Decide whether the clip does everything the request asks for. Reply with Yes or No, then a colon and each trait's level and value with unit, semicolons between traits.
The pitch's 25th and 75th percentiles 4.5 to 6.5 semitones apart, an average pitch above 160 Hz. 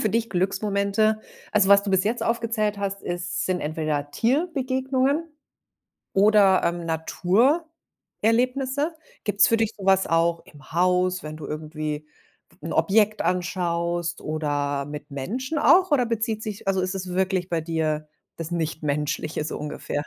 Yes: wide, 5.5 semitones; high, 190 Hz